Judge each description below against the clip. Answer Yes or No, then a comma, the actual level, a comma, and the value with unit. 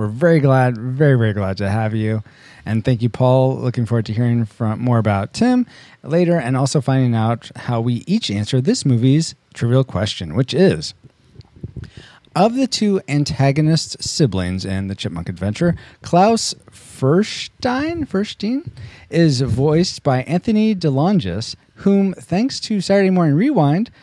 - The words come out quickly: No, average, 145 wpm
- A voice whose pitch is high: No, low, 135 Hz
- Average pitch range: No, wide, 7.5 semitones